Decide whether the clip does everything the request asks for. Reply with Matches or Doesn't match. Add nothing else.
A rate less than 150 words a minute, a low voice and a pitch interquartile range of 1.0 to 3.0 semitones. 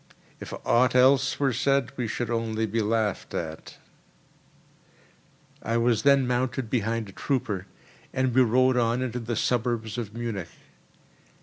Matches